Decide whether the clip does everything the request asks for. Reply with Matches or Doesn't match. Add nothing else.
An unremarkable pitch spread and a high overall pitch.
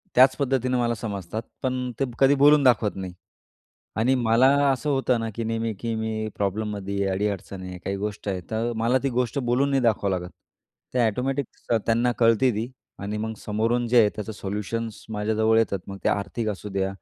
Doesn't match